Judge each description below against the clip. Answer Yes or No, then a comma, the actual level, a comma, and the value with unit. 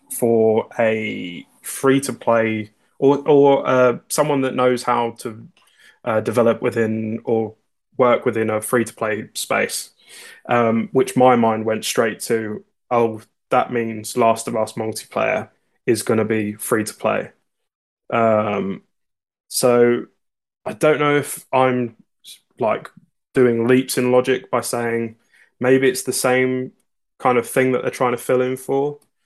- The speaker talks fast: No, average, 150 wpm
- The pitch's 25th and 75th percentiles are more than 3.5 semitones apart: No, narrow, 2.4 semitones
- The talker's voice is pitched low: Yes, low, 120 Hz